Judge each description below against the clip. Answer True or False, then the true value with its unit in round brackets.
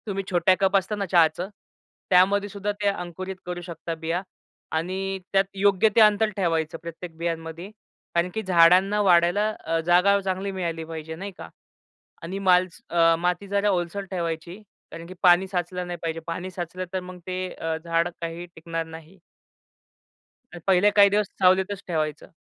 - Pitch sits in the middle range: True (180 Hz)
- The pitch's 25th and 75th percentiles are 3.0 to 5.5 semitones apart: False (2.5 semitones)